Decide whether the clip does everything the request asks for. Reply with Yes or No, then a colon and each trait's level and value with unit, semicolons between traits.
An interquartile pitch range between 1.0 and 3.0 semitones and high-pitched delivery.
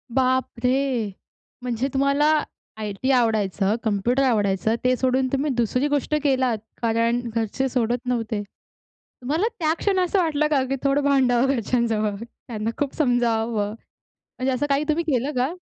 No: average, 3.4 semitones; very high, 250 Hz